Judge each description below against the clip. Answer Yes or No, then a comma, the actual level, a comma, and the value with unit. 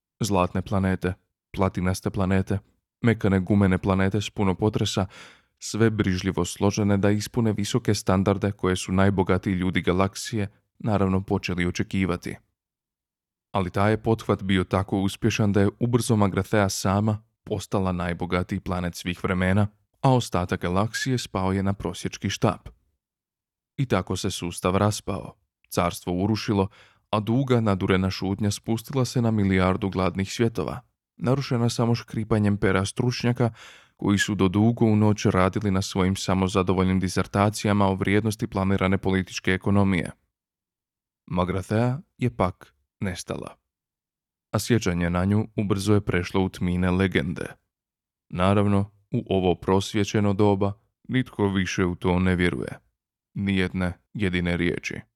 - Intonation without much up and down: Yes, narrow, 2.3 semitones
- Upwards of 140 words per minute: No, average, 125 wpm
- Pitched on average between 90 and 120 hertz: Yes, low, 100 Hz